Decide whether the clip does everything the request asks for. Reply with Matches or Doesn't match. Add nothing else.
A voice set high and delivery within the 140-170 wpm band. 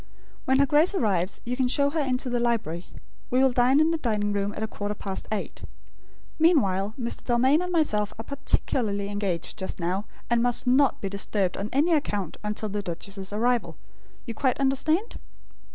Doesn't match